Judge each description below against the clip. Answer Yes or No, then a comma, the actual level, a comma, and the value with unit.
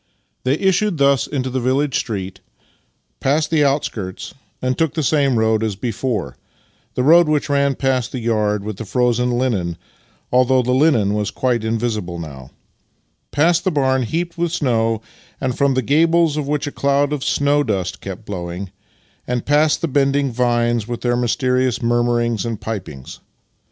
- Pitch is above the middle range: No, low, 125 Hz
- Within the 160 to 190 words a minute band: Yes, average, 165 wpm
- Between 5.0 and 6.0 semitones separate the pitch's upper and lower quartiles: No, average, 4.2 semitones